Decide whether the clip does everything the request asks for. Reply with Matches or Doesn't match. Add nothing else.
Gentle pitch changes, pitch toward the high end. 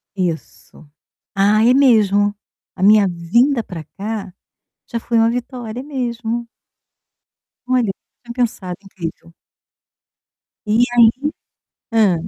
Doesn't match